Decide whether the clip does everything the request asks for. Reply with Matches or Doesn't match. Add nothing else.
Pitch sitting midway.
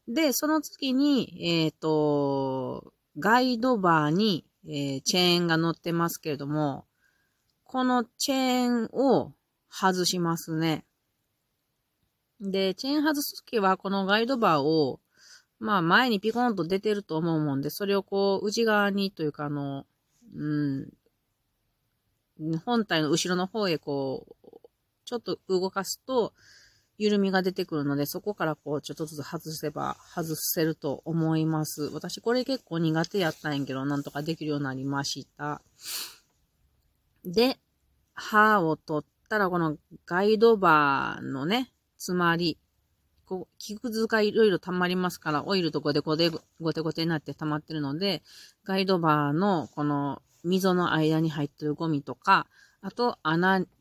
Matches